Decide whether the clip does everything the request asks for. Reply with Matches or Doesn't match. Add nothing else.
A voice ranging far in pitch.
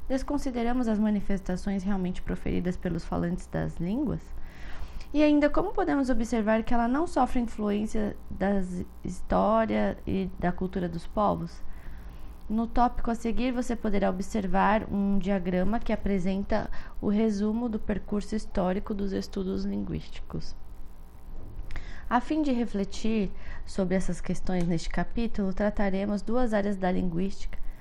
Doesn't match